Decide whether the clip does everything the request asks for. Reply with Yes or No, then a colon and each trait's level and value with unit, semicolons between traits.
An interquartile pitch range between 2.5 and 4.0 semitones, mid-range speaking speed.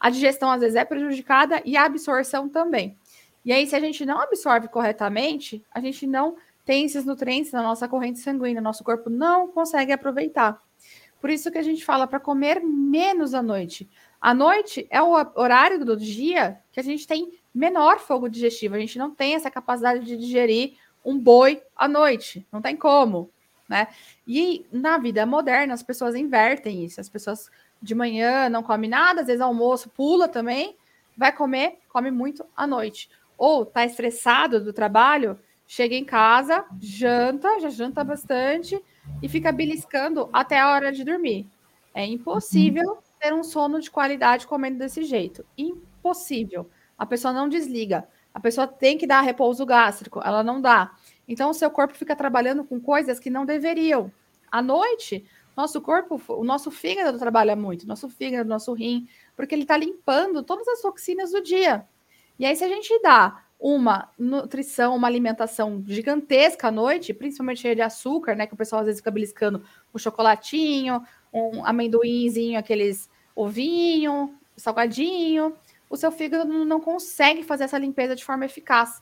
No: average, 4.5 semitones; average, 170 wpm